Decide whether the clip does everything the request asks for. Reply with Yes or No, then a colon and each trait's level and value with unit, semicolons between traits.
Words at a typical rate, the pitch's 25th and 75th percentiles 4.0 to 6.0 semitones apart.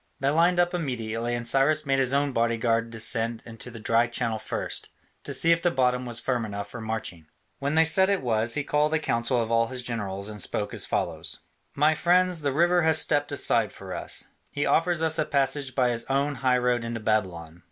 No: fast, 215 wpm; average, 4.6 semitones